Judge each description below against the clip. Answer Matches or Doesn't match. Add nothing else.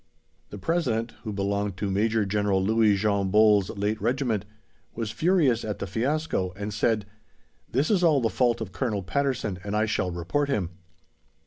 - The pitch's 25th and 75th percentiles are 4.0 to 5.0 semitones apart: Doesn't match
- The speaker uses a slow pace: Doesn't match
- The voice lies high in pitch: Doesn't match